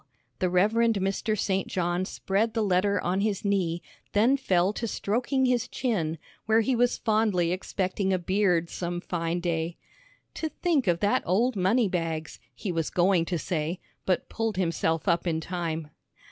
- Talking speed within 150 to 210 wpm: Yes, average, 165 wpm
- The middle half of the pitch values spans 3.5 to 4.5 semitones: Yes, average, 3.8 semitones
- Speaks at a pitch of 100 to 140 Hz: No, high, 190 Hz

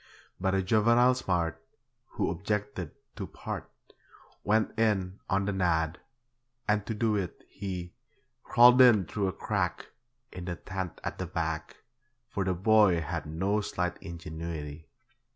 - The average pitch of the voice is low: Yes, very low, 95 Hz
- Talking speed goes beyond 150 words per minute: No, average, 140 wpm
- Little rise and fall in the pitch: No, average, 3.6 semitones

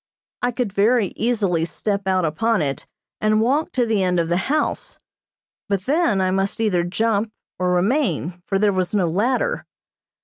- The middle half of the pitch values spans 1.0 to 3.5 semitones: No, average, 4.2 semitones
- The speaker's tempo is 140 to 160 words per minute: No, average, 170 wpm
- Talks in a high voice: Yes, high, 200 Hz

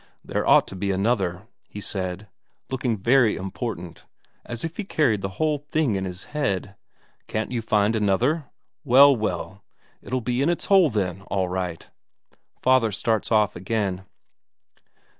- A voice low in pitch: Yes, low, 110 Hz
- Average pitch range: Yes, average, 5.0 semitones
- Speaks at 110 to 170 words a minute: Yes, average, 150 wpm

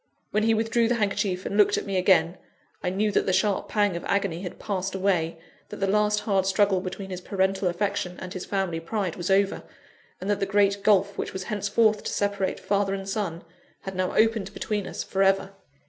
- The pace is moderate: No, fast, 215 wpm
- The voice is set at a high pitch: Yes, high, 195 Hz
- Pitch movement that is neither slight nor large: No, narrow, 1.7 semitones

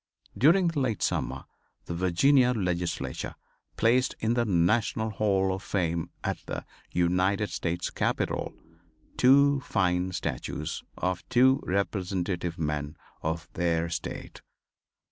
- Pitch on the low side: Yes, very low, 95 Hz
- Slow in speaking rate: Yes, slow, 115 wpm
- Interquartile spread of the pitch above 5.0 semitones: Yes, wide, 5.4 semitones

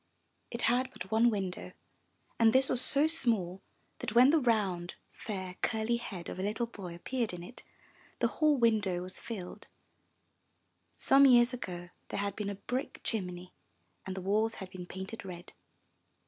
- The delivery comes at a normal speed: Yes, average, 165 wpm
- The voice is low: No, high, 210 Hz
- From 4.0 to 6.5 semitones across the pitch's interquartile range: Yes, average, 4.5 semitones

